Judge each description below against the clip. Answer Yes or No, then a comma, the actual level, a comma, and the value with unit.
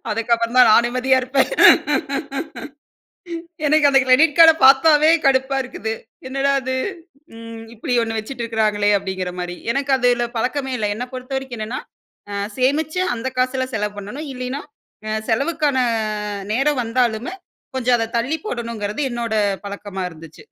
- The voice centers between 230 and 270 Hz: Yes, very high, 250 Hz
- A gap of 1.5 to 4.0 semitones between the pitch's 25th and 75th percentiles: Yes, average, 3.3 semitones